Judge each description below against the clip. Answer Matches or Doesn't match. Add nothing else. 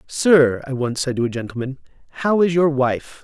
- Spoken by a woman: Doesn't match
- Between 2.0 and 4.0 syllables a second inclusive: Doesn't match